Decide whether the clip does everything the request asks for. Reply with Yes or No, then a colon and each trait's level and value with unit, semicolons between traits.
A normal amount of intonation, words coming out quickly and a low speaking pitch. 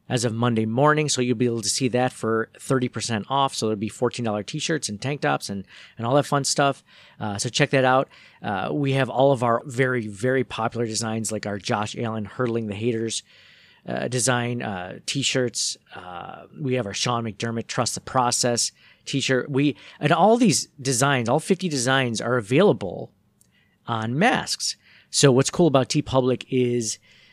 No: average, 3.5 semitones; average, 185 wpm; low, 125 Hz